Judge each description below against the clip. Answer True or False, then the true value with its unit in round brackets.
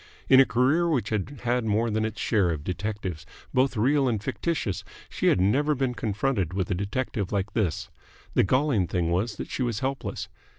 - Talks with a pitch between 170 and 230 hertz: False (110 Hz)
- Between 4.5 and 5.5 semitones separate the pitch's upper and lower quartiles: True (5.1 semitones)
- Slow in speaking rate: False (195 wpm)